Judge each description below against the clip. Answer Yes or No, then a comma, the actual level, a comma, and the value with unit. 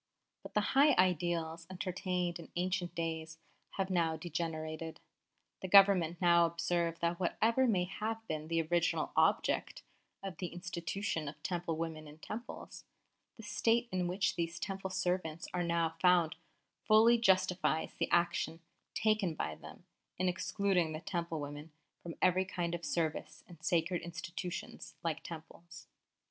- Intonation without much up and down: Yes, narrow, 2.3 semitones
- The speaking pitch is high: No, medium, 175 Hz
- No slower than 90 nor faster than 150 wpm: Yes, average, 145 wpm